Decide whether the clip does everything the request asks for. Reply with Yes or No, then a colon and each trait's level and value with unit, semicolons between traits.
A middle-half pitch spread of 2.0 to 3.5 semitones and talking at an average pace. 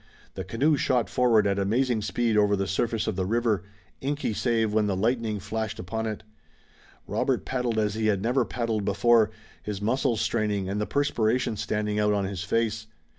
Yes: narrow, 2.4 semitones; average, 180 wpm